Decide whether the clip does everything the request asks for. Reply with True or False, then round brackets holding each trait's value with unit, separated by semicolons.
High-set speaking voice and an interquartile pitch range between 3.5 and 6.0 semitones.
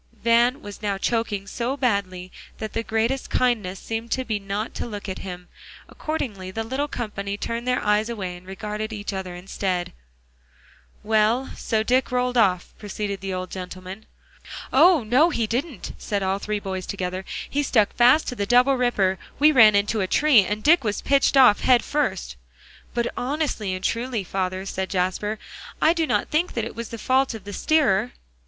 True (215 Hz; 4.3 semitones)